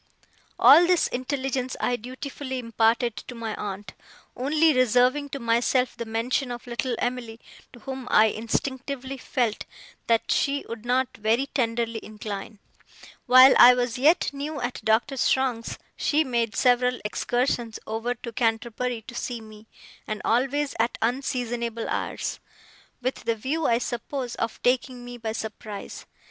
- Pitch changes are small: Yes, narrow, 2.3 semitones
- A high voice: Yes, high, 245 Hz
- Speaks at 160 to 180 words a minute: No, average, 145 wpm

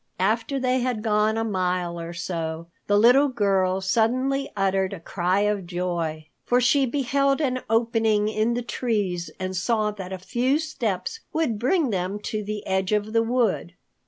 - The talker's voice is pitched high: Yes, high, 210 Hz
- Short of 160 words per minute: No, average, 170 wpm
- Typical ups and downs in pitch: Yes, average, 4.7 semitones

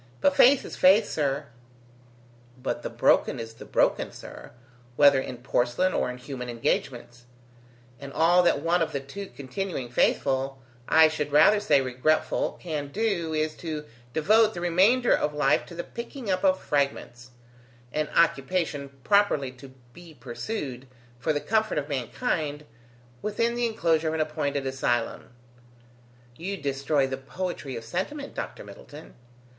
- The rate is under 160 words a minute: Yes, average, 150 wpm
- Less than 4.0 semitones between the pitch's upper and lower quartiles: No, wide, 5.4 semitones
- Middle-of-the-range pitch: Yes, medium, 150 Hz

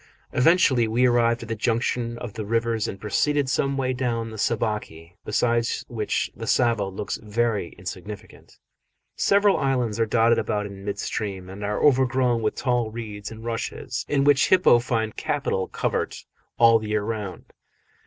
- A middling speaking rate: Yes, average, 165 wpm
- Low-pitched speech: Yes, low, 115 Hz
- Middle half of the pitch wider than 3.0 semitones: No, average, 2.7 semitones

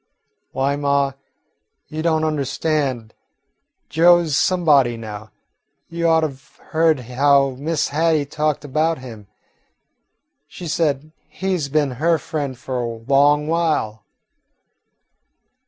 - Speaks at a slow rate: Yes, slow, 120 wpm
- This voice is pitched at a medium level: Yes, medium, 145 Hz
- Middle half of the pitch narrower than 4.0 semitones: Yes, average, 3.3 semitones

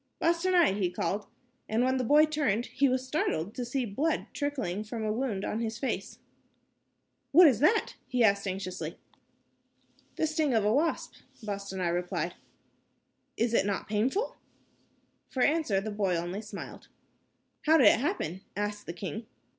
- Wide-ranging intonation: Yes, wide, 6.2 semitones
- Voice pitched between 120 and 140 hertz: No, high, 225 Hz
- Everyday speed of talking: Yes, average, 155 wpm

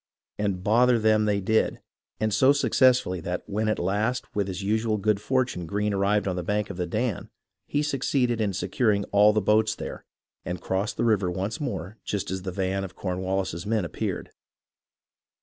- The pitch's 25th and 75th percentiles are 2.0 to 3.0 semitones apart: Yes, average, 2.7 semitones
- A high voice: No, low, 105 Hz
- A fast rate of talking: No, average, 185 wpm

